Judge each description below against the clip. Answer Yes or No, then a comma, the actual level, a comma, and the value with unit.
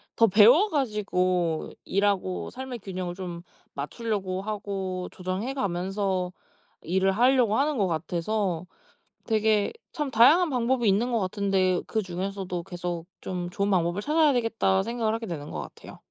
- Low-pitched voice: No, high, 195 Hz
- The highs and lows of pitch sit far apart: No, average, 3.9 semitones